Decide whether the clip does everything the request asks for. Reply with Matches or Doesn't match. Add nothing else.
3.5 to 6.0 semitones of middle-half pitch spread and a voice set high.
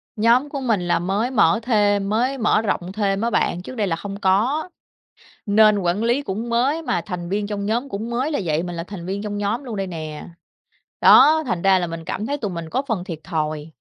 Matches